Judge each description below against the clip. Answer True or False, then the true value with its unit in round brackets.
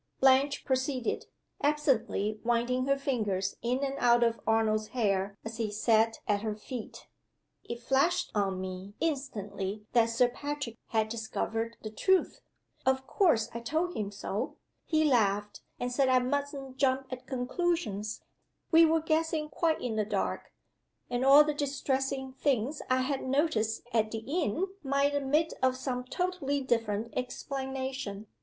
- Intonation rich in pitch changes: False (4.2 semitones)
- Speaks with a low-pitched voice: False (255 Hz)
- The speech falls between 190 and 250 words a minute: False (150 wpm)